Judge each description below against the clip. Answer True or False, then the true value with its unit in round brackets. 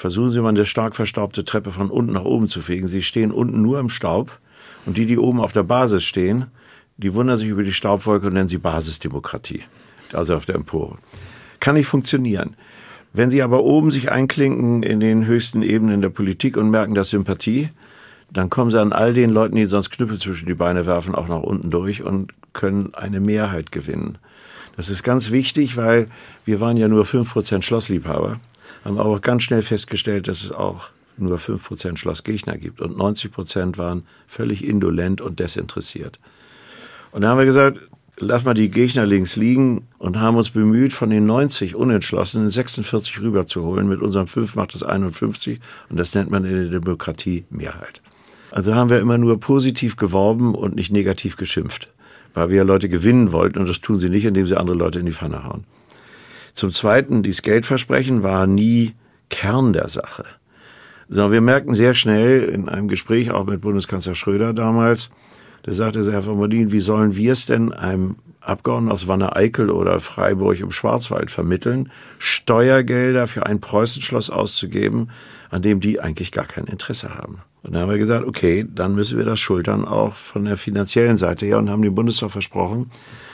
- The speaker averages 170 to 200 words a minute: True (185 wpm)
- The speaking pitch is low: True (105 Hz)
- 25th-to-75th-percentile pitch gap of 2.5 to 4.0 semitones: True (3.4 semitones)